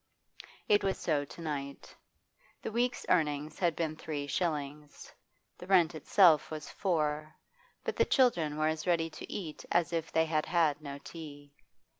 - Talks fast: No, average, 160 wpm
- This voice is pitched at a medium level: Yes, medium, 155 Hz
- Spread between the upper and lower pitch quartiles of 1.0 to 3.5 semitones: Yes, narrow, 2.6 semitones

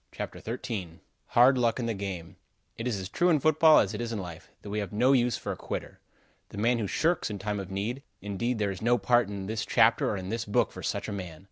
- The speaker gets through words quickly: Yes, fast, 260 wpm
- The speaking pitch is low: Yes, low, 110 Hz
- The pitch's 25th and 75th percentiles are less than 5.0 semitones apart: Yes, average, 3.7 semitones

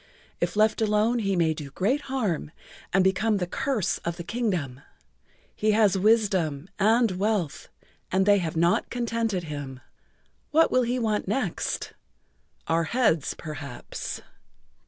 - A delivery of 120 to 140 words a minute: Yes, slow, 135 wpm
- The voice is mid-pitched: No, high, 200 Hz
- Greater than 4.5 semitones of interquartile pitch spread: Yes, average, 5.1 semitones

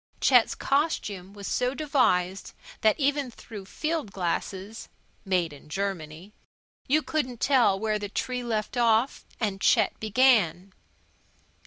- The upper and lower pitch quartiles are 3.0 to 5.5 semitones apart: Yes, average, 4.8 semitones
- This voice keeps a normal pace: No, slow, 120 wpm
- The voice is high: Yes, high, 215 Hz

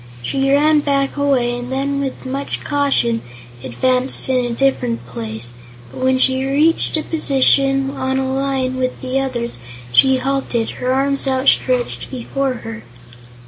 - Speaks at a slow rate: No, average, 150 wpm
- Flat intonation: Yes, narrow, 1.6 semitones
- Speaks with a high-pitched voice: Yes, very high, 265 Hz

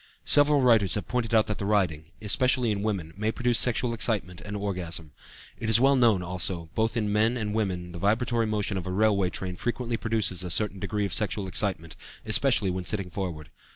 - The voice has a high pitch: No, low, 105 Hz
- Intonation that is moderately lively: Yes, average, 3.6 semitones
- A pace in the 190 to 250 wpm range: Yes, average, 200 wpm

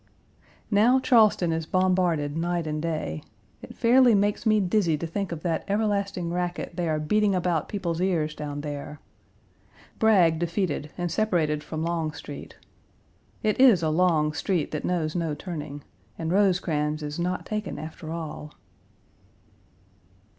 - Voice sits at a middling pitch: Yes, medium, 170 Hz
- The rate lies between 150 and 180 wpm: No, average, 140 wpm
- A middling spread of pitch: Yes, average, 4.0 semitones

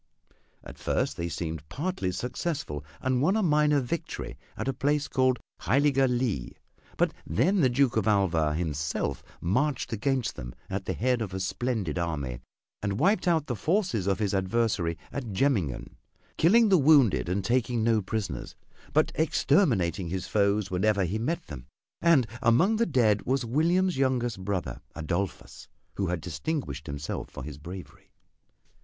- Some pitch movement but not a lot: No, wide, 7.5 semitones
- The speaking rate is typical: Yes, average, 155 wpm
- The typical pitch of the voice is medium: No, low, 110 Hz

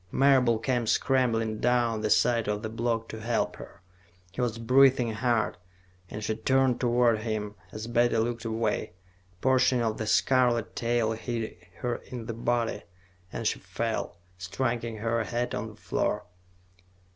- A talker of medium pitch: No, low, 115 Hz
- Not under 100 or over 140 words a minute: No, average, 155 wpm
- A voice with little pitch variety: Yes, narrow, 1.8 semitones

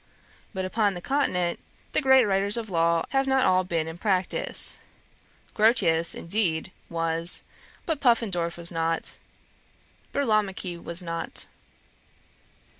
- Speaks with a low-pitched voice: No, medium, 185 Hz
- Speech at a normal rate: No, slow, 115 wpm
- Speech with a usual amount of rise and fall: Yes, average, 4.7 semitones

